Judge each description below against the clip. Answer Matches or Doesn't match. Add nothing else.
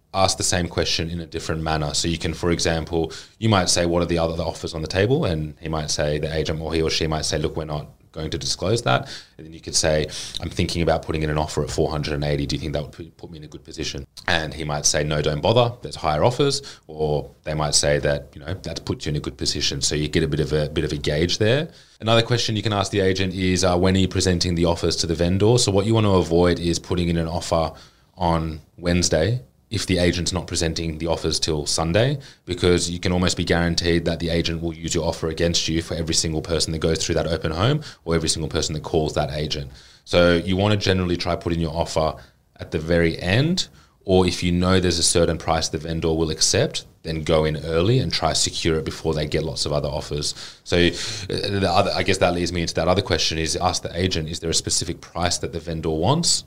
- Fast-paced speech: Matches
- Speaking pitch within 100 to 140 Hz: Doesn't match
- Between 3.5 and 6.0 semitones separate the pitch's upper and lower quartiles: Doesn't match